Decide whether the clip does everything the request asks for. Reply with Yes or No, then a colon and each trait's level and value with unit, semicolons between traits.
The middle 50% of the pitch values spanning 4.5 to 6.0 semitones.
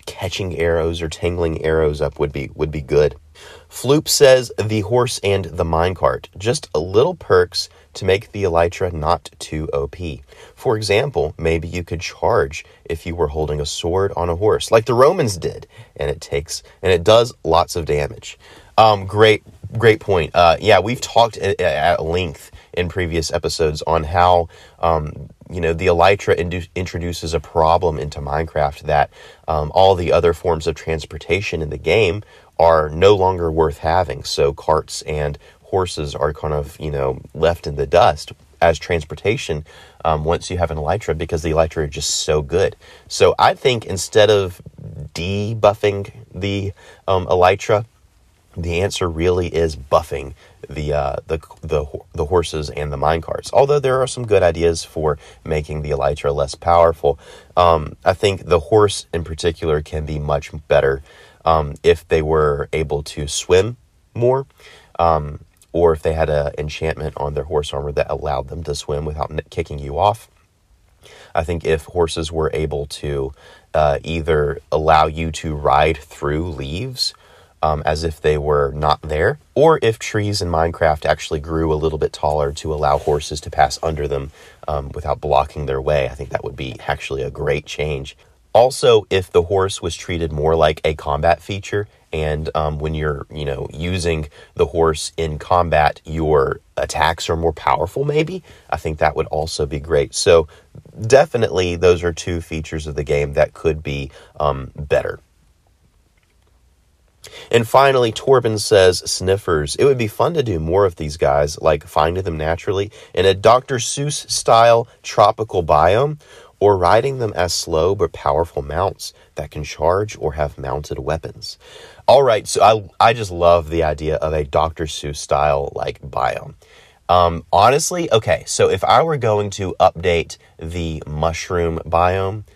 No: average, 3.6 semitones